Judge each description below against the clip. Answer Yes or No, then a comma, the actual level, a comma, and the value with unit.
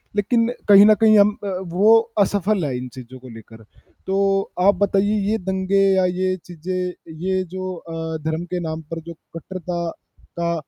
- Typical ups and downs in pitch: Yes, average, 3.4 semitones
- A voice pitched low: No, medium, 185 Hz